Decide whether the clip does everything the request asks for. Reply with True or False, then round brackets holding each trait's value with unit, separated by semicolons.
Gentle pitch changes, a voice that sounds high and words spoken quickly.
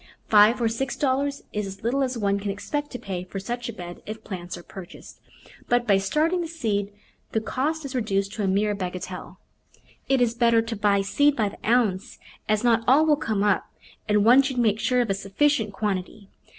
False (4.2 semitones; 220 Hz; 210 wpm)